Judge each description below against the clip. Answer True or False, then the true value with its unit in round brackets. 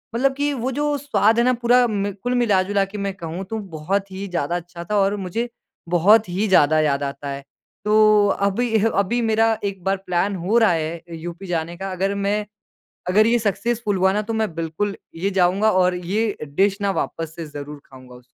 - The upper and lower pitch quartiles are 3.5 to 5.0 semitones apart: True (3.9 semitones)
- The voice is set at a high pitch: True (195 Hz)